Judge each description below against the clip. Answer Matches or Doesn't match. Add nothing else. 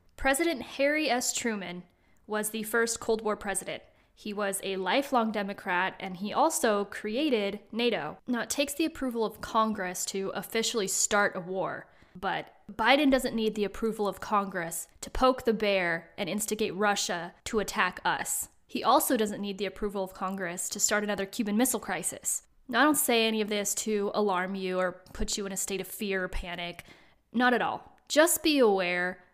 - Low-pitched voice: Doesn't match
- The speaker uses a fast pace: Doesn't match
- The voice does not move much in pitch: Doesn't match